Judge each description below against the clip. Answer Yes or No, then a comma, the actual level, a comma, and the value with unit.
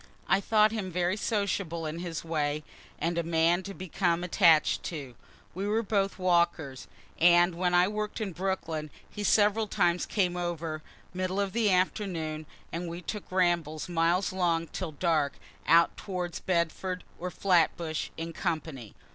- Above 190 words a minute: No, average, 150 wpm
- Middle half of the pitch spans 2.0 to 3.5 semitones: Yes, narrow, 2.6 semitones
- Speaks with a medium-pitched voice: Yes, medium, 175 Hz